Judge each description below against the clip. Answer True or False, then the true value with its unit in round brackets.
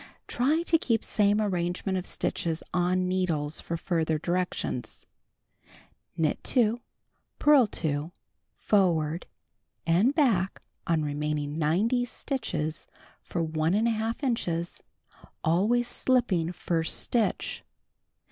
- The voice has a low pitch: False (180 Hz)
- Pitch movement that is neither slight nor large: False (5.9 semitones)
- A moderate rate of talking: False (100 wpm)